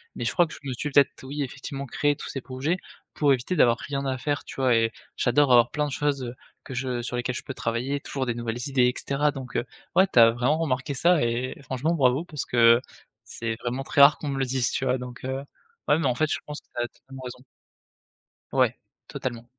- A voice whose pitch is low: Yes, low, 130 Hz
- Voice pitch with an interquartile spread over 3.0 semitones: No, average, 2.7 semitones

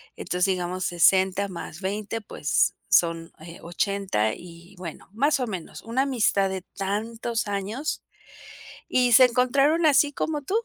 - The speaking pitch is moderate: No, high, 200 Hz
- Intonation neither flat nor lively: No, wide, 5.7 semitones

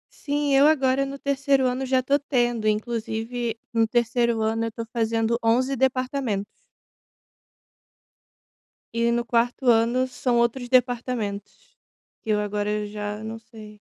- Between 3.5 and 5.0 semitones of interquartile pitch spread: No, average, 2.7 semitones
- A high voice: Yes, high, 235 Hz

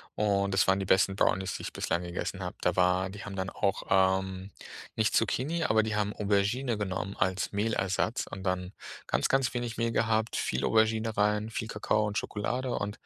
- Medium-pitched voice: No, low, 100 Hz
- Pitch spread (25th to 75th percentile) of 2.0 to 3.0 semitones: Yes, average, 2.7 semitones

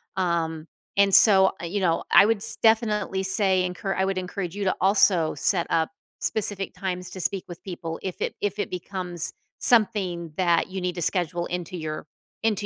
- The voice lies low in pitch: No, medium, 185 Hz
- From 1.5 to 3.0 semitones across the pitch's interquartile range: Yes, narrow, 2.4 semitones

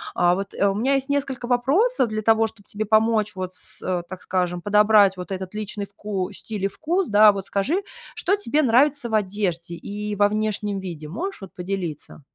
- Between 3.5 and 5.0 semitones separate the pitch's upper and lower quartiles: No, average, 3.0 semitones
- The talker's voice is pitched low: No, high, 205 Hz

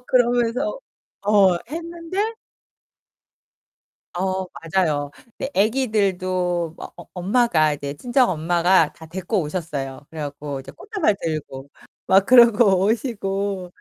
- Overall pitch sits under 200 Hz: Yes, high, 190 Hz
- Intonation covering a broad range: Yes, wide, 6.5 semitones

